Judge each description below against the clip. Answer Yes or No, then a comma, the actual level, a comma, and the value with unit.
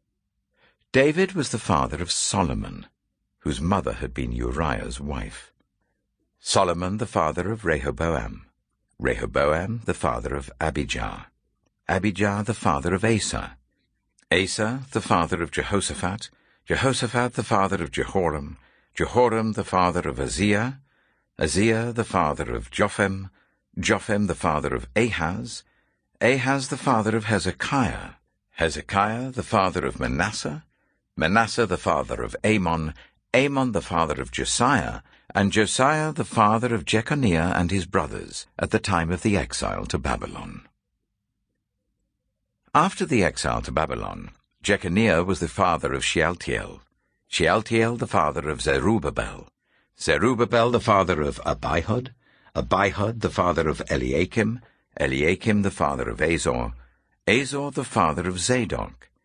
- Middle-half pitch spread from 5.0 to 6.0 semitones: Yes, wide, 5.4 semitones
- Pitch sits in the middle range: No, low, 100 Hz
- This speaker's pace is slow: Yes, slow, 125 wpm